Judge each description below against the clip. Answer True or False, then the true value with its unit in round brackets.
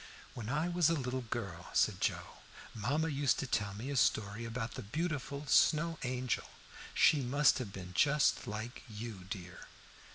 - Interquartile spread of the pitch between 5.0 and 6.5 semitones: True (5.3 semitones)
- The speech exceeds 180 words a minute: False (165 wpm)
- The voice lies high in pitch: False (125 Hz)